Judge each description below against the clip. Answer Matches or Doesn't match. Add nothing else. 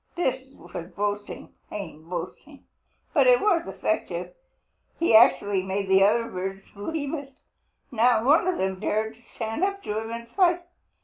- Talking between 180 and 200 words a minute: Doesn't match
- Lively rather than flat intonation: Matches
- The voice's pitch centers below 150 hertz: Doesn't match